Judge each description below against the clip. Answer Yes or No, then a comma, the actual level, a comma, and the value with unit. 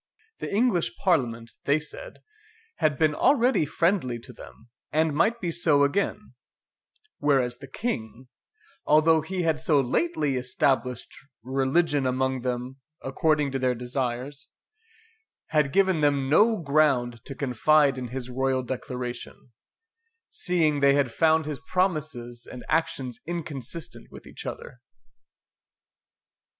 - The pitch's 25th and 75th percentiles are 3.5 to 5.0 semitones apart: Yes, average, 4.1 semitones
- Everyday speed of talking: No, slow, 125 wpm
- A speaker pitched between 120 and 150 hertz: Yes, medium, 140 Hz